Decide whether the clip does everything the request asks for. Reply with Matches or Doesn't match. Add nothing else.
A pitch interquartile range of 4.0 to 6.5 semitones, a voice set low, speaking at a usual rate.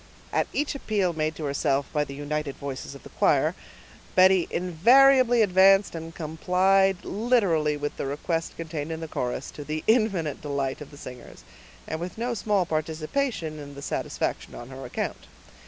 Doesn't match